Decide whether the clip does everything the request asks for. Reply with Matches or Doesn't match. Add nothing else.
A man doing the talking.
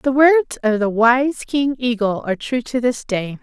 Doesn't match